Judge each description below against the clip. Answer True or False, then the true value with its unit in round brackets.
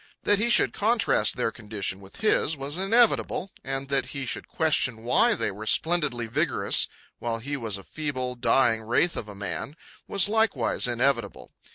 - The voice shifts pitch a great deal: True (7.2 semitones)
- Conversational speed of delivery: True (170 wpm)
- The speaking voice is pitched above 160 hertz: False (135 Hz)